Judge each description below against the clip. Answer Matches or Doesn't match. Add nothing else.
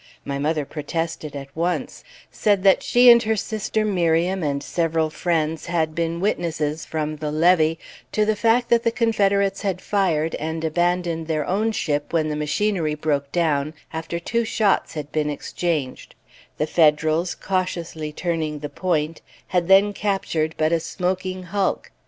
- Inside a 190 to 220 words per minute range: Doesn't match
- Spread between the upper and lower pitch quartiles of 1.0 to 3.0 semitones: Doesn't match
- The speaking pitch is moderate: Matches